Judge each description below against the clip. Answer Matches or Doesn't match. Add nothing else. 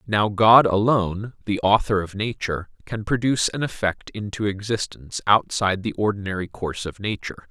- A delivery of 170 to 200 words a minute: Doesn't match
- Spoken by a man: Matches